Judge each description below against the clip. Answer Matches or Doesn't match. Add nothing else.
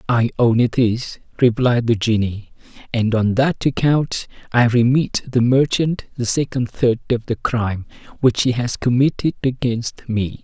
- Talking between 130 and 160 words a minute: Matches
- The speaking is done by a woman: Doesn't match